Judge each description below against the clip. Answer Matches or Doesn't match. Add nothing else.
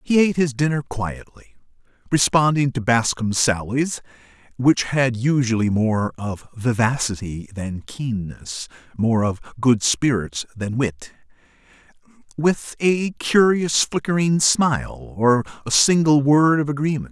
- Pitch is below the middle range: Matches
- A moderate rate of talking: Doesn't match